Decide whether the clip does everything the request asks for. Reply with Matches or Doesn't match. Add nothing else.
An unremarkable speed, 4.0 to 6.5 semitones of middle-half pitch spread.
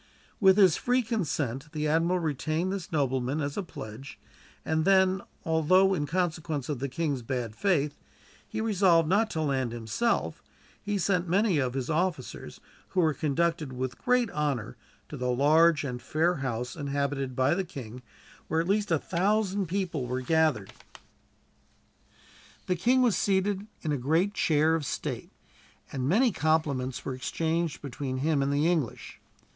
Matches